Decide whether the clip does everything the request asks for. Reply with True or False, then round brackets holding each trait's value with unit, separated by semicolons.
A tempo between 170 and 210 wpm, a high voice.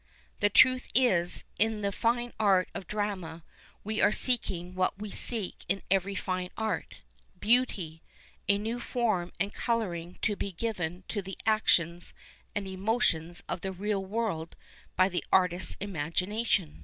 False (155 wpm; 195 Hz)